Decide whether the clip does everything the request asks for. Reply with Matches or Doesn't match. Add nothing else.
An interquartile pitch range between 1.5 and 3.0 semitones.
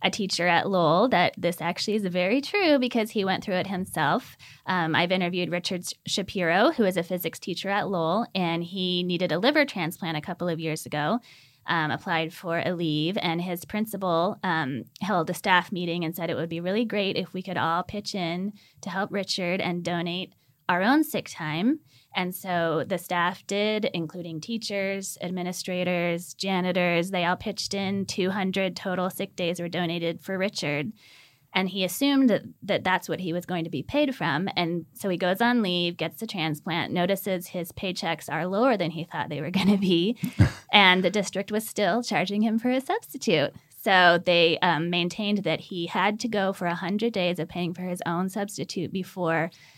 Matches